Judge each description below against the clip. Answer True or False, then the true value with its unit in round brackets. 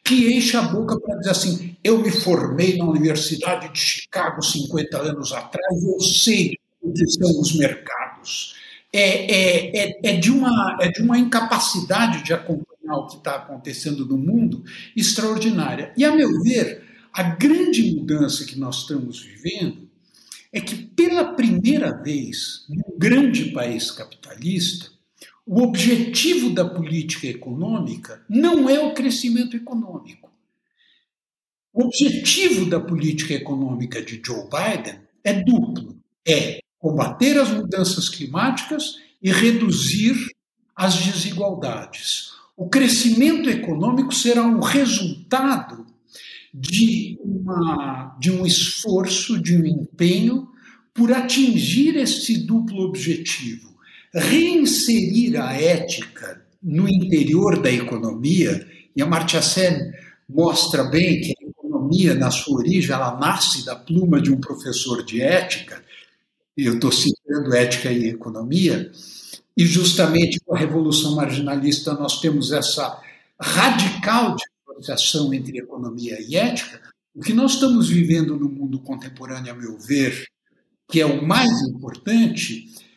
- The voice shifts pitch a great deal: True (7.2 semitones)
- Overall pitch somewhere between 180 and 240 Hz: True (185 Hz)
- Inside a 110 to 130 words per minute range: True (125 wpm)